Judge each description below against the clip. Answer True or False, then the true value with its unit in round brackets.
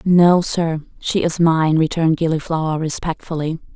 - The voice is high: False (160 Hz)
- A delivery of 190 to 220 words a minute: False (130 wpm)